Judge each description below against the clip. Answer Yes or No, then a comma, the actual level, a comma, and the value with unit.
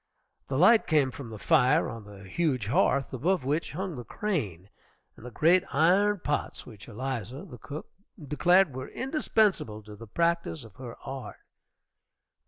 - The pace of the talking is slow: No, average, 160 wpm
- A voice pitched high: No, medium, 140 Hz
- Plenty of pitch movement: Yes, wide, 6.5 semitones